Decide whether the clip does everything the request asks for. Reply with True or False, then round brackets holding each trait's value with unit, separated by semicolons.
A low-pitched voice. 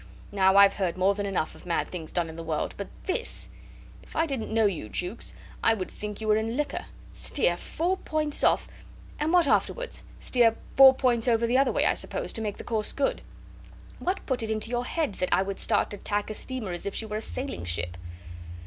False (220 Hz)